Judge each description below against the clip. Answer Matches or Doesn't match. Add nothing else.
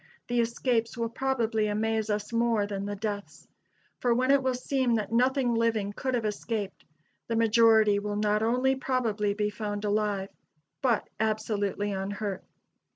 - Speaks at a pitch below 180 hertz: Doesn't match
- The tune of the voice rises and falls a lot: Doesn't match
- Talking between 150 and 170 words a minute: Matches